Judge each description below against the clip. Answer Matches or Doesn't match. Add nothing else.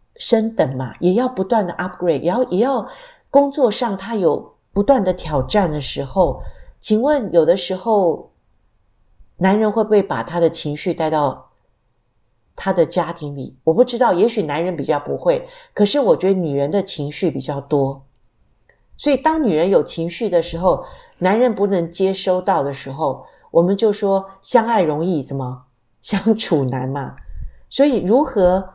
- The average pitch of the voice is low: Doesn't match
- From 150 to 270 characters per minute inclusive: Matches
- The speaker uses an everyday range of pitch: Doesn't match